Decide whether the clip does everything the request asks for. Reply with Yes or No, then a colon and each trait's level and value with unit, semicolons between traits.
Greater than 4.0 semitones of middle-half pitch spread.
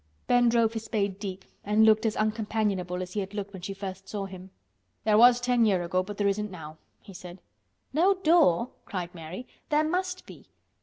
No: average, 3.7 semitones